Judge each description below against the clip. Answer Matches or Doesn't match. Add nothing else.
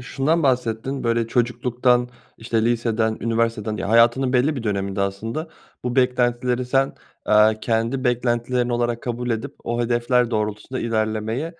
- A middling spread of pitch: Doesn't match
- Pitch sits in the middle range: Doesn't match